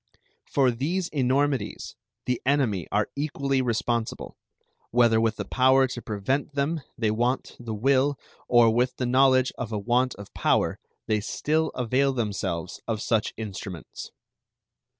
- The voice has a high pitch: No, low, 125 Hz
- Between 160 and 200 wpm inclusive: No, average, 140 wpm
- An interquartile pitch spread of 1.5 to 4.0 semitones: Yes, average, 3.4 semitones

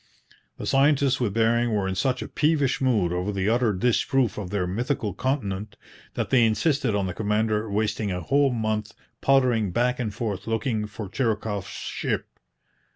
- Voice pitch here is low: Yes, low, 110 Hz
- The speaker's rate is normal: Yes, average, 165 wpm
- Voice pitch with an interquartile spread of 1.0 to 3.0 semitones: No, average, 3.7 semitones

